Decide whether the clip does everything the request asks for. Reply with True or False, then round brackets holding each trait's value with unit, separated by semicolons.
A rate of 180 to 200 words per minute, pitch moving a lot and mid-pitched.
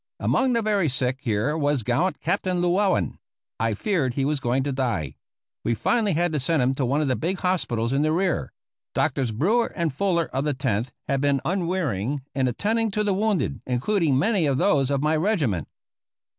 True (195 wpm; 6.3 semitones; 145 Hz)